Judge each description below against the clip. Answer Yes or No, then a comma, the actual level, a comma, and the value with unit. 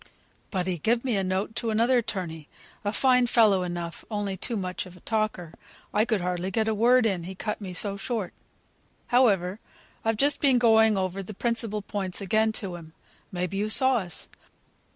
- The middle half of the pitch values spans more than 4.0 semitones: No, average, 3.6 semitones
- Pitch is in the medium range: No, high, 205 Hz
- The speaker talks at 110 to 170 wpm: No, average, 195 wpm